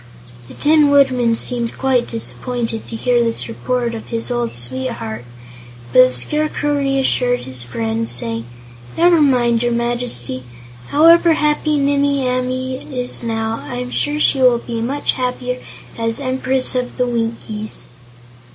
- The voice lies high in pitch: Yes, high, 245 Hz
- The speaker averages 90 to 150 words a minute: Yes, average, 140 wpm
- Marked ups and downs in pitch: No, average, 2.8 semitones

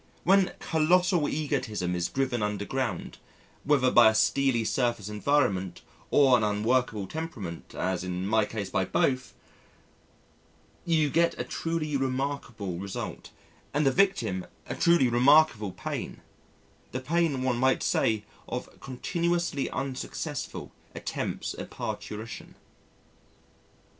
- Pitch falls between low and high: No, low, 130 Hz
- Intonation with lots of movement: Yes, wide, 5.9 semitones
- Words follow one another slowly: Yes, slow, 120 wpm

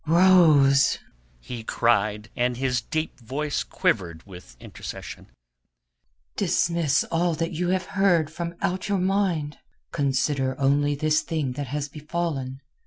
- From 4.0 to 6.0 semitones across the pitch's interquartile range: Yes, average, 4.6 semitones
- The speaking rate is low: Yes, slow, 125 wpm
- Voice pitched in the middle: Yes, medium, 145 Hz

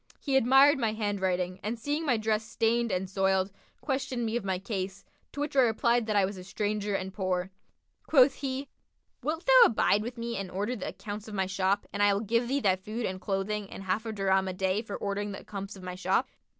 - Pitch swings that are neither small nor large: Yes, average, 3.6 semitones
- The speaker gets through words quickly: Yes, fast, 230 wpm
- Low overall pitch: No, high, 210 Hz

